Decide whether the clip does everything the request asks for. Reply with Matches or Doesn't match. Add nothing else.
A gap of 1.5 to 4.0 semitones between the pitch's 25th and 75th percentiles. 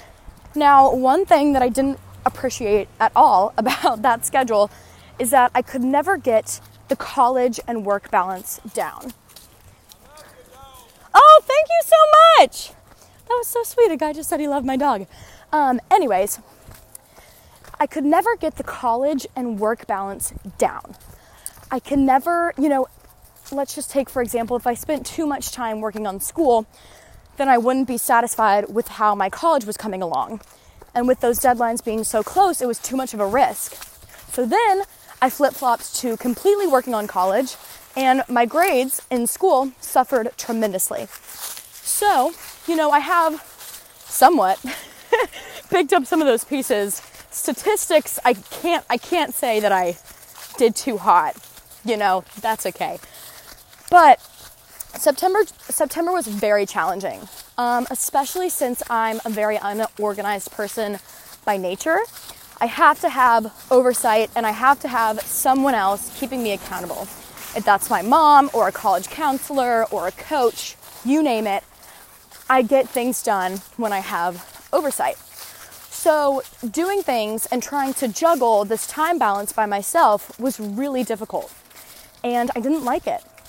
Doesn't match